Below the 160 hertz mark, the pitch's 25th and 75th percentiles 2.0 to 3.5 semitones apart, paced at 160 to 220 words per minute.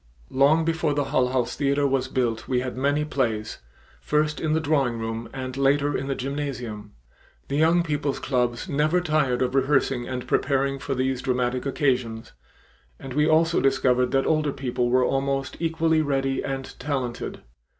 Yes: low, 135 Hz; average, 2.7 semitones; average, 165 wpm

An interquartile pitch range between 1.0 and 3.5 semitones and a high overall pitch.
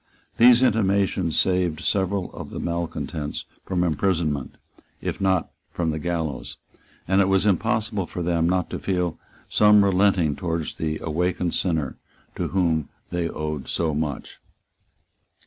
No: average, 3.2 semitones; very low, 90 Hz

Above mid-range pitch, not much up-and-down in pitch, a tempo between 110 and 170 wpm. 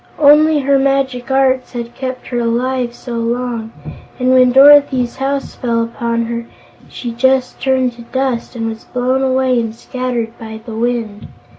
Yes: very high, 250 Hz; narrow, 2.1 semitones; average, 160 wpm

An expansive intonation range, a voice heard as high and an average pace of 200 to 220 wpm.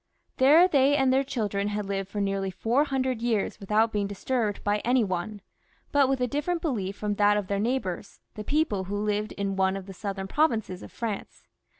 No: average, 4.7 semitones; high, 210 Hz; fast, 205 wpm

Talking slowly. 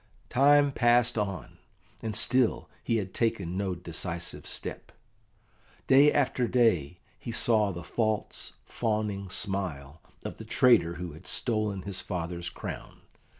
Yes: slow, 130 wpm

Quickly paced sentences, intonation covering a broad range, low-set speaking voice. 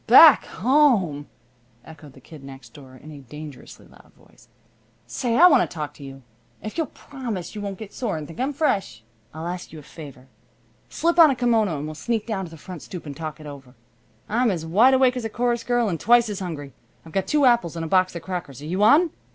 No: fast, 235 wpm; wide, 8.0 semitones; medium, 185 Hz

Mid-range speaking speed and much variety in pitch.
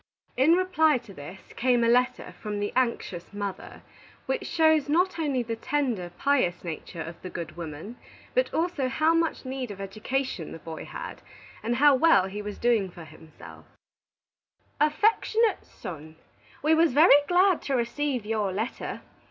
Yes: average, 160 wpm; wide, 7.6 semitones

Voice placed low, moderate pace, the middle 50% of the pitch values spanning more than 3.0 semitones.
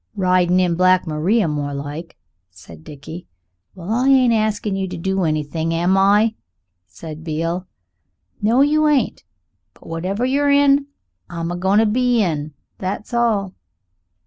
No: medium, 185 Hz; average, 145 wpm; average, 5.2 semitones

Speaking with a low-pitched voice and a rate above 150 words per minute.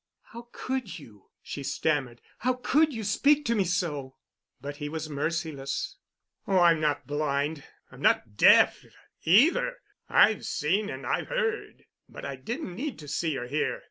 No: medium, 165 Hz; average, 170 wpm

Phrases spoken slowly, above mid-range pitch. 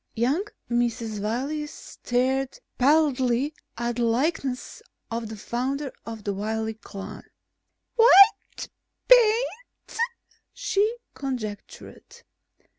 Yes: slow, 90 wpm; very high, 250 Hz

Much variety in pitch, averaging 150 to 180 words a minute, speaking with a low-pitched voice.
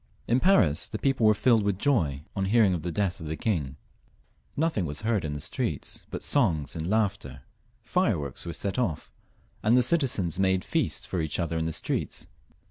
No: wide, 6.2 semitones; average, 200 wpm; very low, 95 Hz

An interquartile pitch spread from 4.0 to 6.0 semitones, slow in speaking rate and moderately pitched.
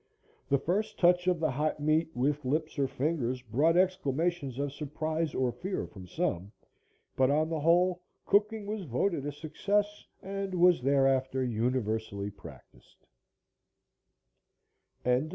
Yes: average, 5.2 semitones; slow, 130 wpm; medium, 150 Hz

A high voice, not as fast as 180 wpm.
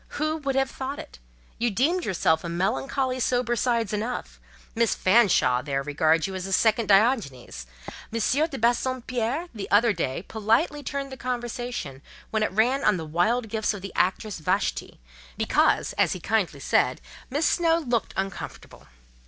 Yes: high, 225 Hz; average, 160 wpm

